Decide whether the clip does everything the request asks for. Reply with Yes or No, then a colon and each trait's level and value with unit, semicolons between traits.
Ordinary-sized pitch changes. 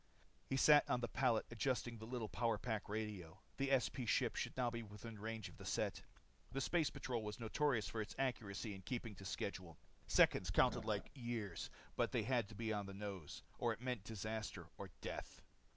Yes: average, 3.2 semitones